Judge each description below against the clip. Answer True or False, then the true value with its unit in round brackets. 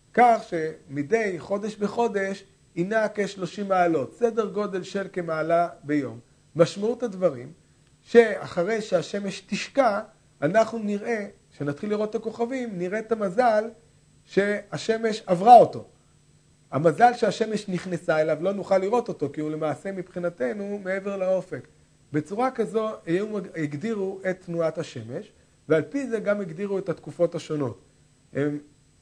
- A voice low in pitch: False (190 Hz)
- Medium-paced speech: True (120 wpm)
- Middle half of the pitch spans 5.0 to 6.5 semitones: True (5.3 semitones)